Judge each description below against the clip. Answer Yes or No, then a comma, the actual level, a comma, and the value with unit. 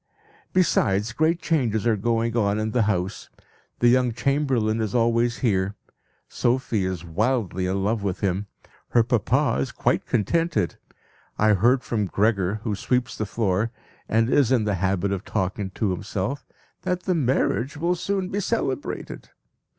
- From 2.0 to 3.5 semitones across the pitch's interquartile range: No, average, 4.4 semitones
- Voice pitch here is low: Yes, low, 115 Hz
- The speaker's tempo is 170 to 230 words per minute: No, average, 155 wpm